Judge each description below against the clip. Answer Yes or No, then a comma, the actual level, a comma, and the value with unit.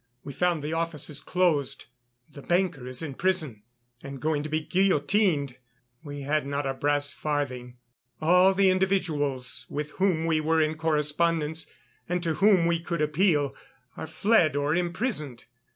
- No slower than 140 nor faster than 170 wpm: Yes, average, 150 wpm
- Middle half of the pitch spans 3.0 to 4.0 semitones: Yes, average, 3.4 semitones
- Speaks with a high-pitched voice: No, medium, 155 Hz